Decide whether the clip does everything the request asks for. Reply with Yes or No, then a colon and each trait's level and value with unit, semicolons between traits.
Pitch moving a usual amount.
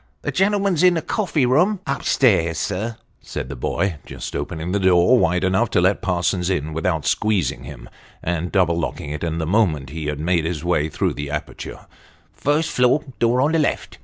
No: wide, 7.6 semitones